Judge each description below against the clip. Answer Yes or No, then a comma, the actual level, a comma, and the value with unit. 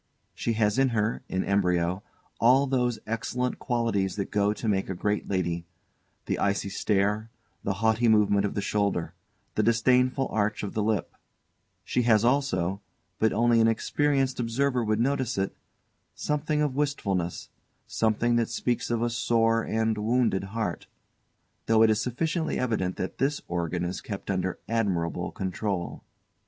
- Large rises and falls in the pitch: No, average, 3.5 semitones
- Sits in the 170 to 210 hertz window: No, low, 110 Hz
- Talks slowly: No, average, 155 wpm